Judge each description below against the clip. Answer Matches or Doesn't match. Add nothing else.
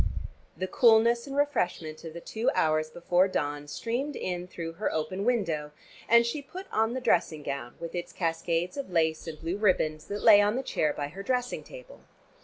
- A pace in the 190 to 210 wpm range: Matches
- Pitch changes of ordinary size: Doesn't match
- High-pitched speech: Doesn't match